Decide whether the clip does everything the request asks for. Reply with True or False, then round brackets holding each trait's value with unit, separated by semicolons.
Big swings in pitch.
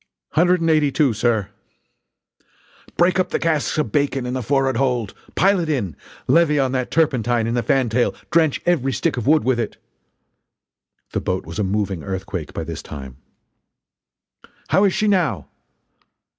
True (5.9 semitones)